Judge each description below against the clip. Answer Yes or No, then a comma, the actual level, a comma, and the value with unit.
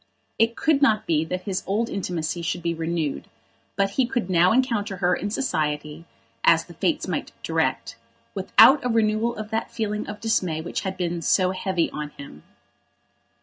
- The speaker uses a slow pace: No, average, 175 wpm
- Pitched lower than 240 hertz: Yes, high, 190 Hz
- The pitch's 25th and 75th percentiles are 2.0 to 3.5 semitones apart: No, average, 4.7 semitones